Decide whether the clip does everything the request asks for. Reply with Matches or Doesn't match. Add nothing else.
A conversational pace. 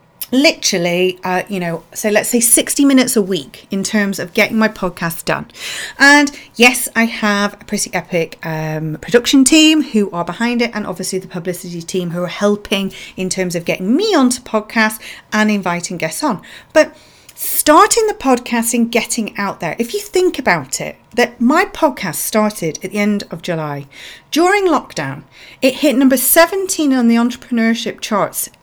Matches